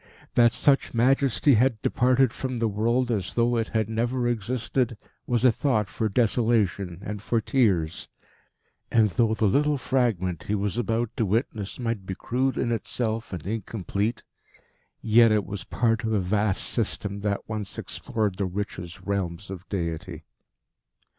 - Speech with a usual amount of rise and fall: Yes, average, 3.2 semitones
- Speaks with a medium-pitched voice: No, low, 110 Hz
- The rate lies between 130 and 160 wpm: Yes, average, 155 wpm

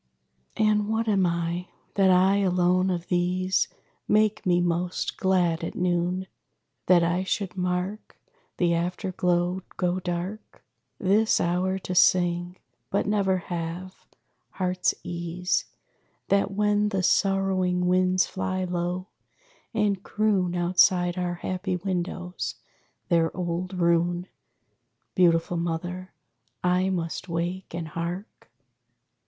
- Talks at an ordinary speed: No, slow, 115 wpm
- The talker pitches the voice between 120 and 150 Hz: No, medium, 180 Hz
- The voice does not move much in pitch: Yes, narrow, 1.4 semitones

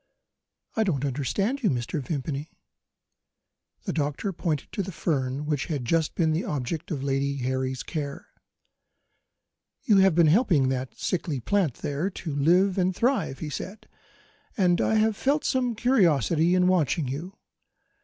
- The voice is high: No, medium, 160 Hz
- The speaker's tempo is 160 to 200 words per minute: No, average, 150 wpm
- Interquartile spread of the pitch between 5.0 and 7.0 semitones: Yes, wide, 5.5 semitones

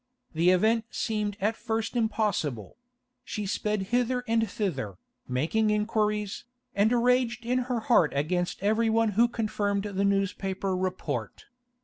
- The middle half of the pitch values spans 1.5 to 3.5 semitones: Yes, average, 3.2 semitones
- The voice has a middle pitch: No, high, 210 Hz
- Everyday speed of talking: No, slow, 125 wpm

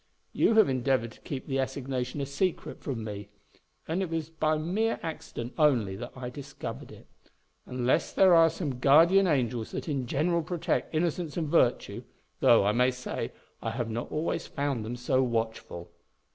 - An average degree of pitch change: Yes, average, 4.9 semitones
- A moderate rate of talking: Yes, average, 175 wpm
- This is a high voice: No, low, 135 Hz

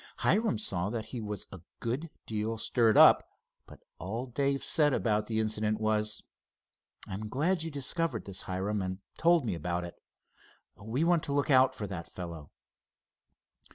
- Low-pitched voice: Yes, low, 110 Hz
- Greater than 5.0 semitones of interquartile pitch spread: Yes, wide, 5.4 semitones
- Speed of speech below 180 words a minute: Yes, average, 160 wpm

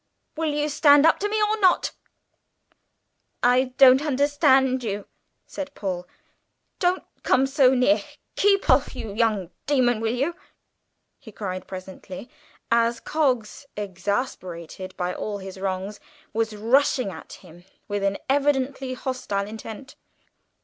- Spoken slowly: Yes, slow, 130 wpm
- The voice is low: No, high, 245 Hz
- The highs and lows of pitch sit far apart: Yes, wide, 6.1 semitones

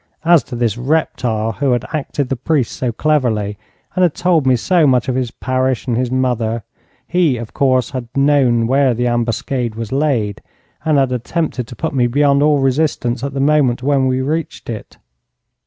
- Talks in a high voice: No, low, 130 Hz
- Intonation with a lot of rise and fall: No, average, 3.2 semitones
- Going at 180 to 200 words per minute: Yes, average, 190 wpm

